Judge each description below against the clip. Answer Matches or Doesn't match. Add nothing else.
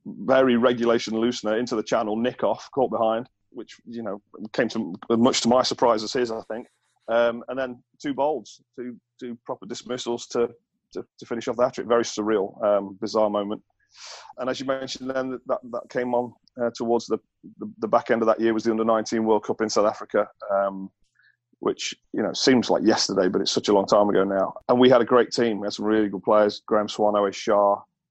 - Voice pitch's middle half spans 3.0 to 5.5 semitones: Doesn't match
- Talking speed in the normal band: Doesn't match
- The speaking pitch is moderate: Doesn't match